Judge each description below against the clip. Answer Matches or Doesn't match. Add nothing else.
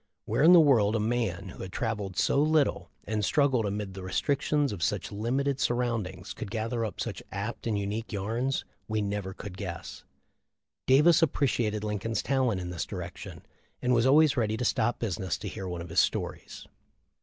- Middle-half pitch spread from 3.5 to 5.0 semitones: Matches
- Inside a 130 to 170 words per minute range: Doesn't match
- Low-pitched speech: Matches